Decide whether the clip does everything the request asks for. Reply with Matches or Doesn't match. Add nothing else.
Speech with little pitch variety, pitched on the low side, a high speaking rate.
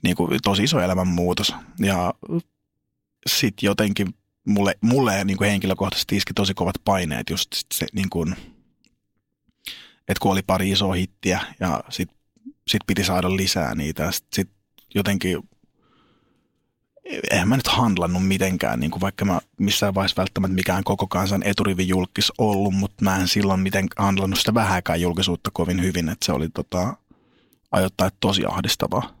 Doesn't match